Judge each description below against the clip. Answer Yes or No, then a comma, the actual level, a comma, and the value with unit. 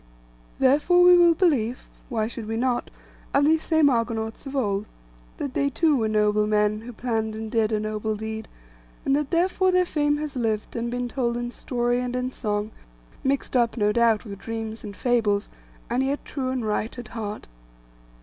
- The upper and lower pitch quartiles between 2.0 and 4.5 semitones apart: Yes, average, 3.9 semitones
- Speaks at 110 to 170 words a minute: No, average, 180 wpm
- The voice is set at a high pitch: Yes, high, 235 Hz